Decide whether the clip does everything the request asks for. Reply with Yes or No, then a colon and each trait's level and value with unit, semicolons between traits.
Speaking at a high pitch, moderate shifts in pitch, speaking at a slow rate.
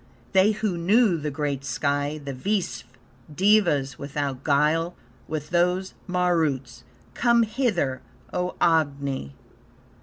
No: medium, 160 Hz; average, 4.9 semitones; slow, 110 wpm